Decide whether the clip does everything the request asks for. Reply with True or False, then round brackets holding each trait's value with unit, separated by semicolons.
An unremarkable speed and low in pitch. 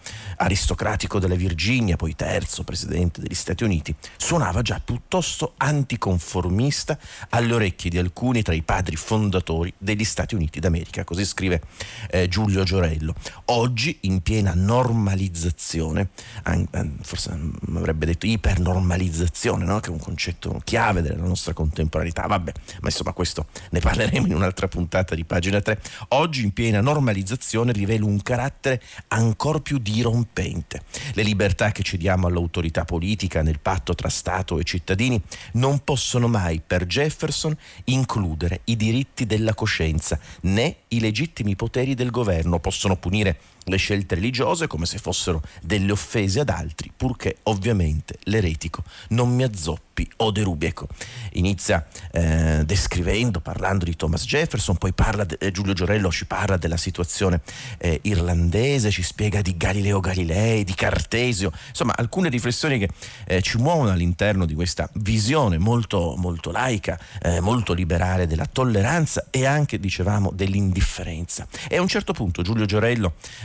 True (140 wpm; 95 Hz)